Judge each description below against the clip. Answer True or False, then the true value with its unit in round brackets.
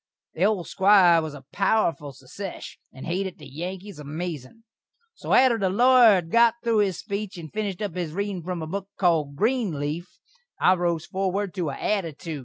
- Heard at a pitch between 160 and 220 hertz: True (185 Hz)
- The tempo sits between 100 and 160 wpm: False (180 wpm)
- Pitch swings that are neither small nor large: True (4.0 semitones)